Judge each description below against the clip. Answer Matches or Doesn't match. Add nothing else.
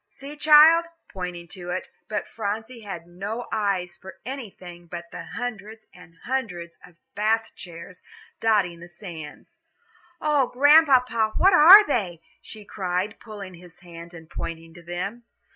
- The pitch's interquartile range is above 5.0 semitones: Matches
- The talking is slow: Doesn't match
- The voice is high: Matches